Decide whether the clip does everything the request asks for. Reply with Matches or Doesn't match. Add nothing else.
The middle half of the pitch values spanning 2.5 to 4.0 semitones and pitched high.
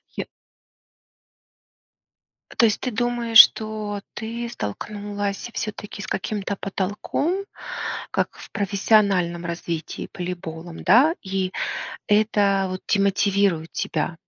Matches